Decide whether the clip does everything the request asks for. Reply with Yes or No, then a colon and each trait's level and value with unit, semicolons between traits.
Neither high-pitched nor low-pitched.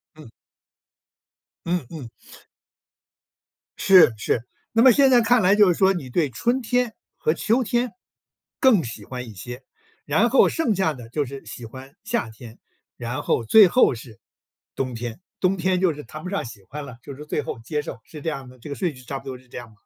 Yes: medium, 150 Hz